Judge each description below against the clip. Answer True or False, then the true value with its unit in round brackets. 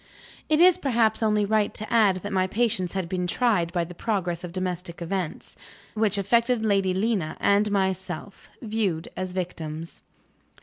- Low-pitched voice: False (195 Hz)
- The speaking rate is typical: True (160 wpm)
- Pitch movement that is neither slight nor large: True (3.4 semitones)